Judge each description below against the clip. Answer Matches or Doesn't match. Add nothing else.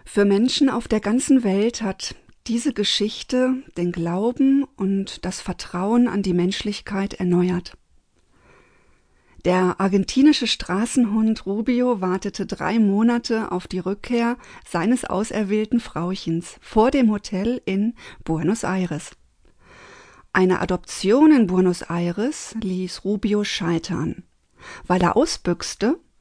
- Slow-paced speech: Matches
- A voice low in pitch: Doesn't match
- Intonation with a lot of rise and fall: Doesn't match